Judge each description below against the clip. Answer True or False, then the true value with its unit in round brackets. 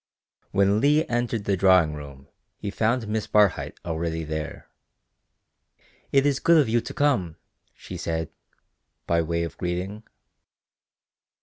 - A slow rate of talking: True (130 wpm)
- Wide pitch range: True (6.0 semitones)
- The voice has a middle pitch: False (95 Hz)